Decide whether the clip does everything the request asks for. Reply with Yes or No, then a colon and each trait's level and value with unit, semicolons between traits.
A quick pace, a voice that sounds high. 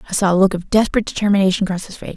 Yes: fast, 280 wpm; high, 195 Hz